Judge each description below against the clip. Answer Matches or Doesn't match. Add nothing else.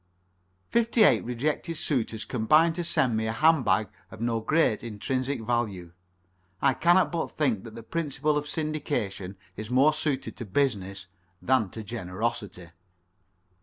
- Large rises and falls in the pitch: Matches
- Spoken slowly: Doesn't match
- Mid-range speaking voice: Doesn't match